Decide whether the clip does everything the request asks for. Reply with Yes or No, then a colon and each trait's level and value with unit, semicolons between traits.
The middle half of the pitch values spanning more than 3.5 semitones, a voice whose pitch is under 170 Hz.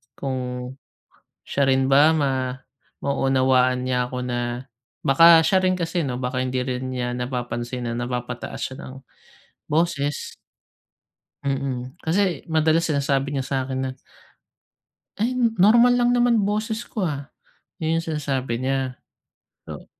Yes: average, 4.3 semitones; low, 135 Hz